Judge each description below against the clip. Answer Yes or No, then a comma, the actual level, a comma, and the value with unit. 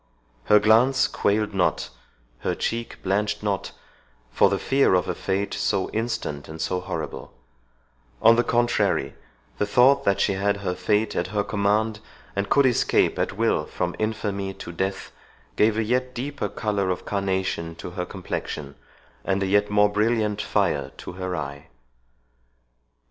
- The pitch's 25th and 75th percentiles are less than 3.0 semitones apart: Yes, narrow, 2.6 semitones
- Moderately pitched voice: No, low, 100 Hz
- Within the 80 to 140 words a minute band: No, average, 155 wpm